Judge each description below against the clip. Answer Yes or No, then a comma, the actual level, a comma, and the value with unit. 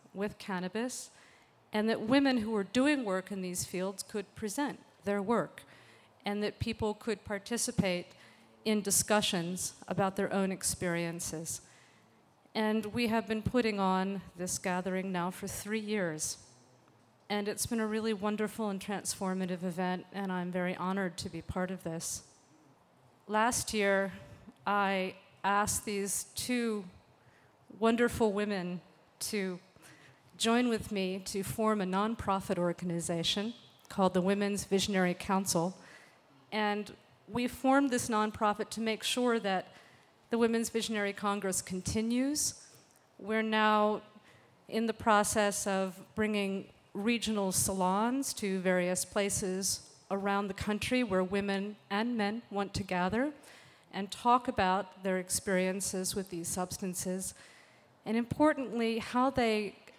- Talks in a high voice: Yes, high, 200 Hz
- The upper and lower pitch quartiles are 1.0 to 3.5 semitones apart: Yes, average, 2.8 semitones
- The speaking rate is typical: No, slow, 125 wpm